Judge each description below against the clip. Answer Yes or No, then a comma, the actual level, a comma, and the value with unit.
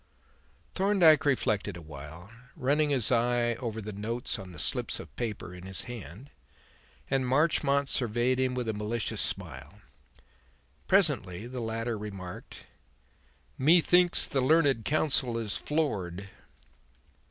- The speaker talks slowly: Yes, slow, 125 wpm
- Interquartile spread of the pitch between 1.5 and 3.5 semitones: No, wide, 5.5 semitones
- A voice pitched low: Yes, low, 120 Hz